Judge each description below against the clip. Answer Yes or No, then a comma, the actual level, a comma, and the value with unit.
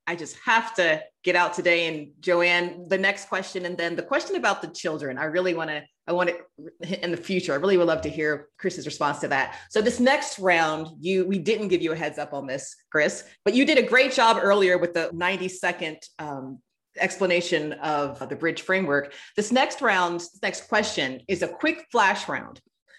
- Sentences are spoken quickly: Yes, fast, 210 wpm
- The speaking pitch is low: No, medium, 175 Hz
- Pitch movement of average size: Yes, average, 3.3 semitones